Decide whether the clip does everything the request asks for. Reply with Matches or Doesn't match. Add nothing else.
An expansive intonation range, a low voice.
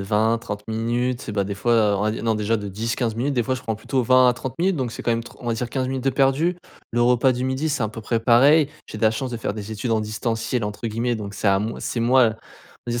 Doesn't match